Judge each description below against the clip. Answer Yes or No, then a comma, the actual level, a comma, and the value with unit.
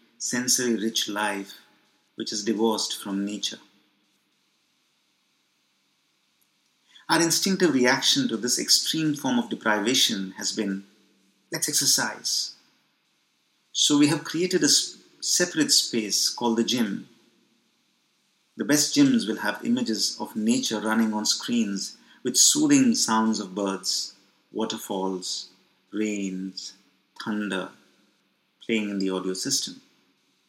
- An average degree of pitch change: No, wide, 6.8 semitones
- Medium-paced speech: No, slow, 110 wpm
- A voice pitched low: Yes, low, 110 Hz